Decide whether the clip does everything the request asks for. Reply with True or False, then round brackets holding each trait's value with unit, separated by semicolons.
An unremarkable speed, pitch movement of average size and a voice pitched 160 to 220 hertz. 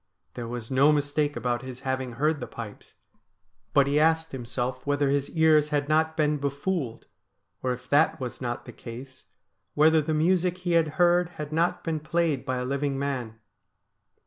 False (175 wpm; 3.5 semitones; 145 Hz)